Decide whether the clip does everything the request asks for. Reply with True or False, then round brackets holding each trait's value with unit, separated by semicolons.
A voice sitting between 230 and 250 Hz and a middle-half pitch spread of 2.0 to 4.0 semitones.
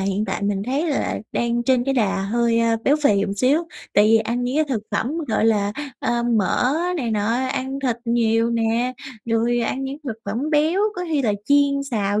True (235 Hz; 3.7 semitones)